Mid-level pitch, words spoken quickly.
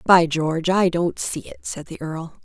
Yes: medium, 165 Hz; fast, 220 wpm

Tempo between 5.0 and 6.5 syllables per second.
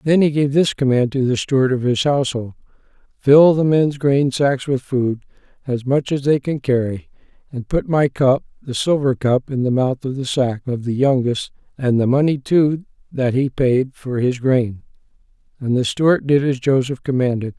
No: 4.8 syllables/s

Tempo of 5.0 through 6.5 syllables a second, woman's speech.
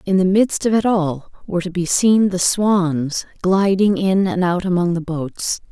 No: 4.3 syllables/s; female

